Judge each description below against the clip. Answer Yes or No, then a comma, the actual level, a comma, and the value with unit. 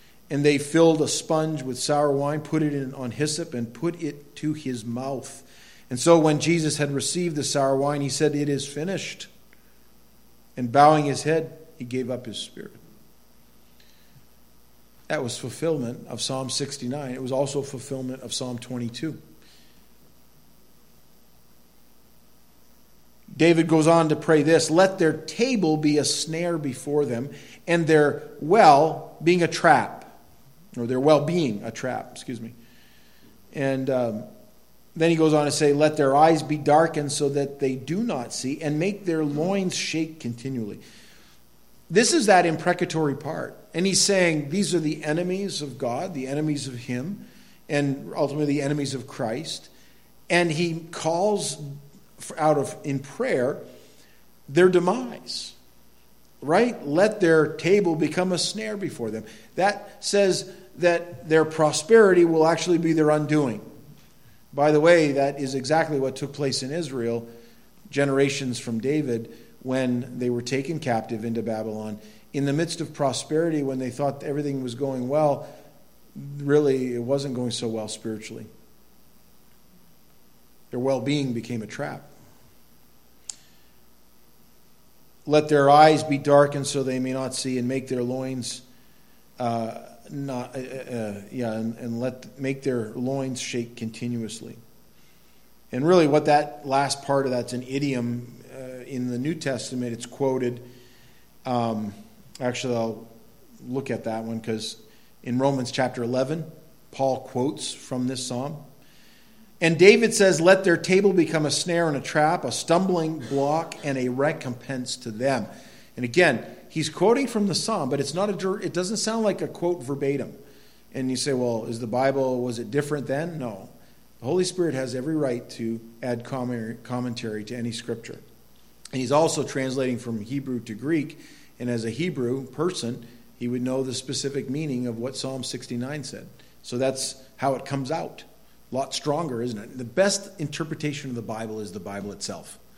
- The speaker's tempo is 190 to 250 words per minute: No, average, 155 wpm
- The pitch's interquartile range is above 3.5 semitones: Yes, average, 4.4 semitones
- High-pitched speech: No, medium, 140 Hz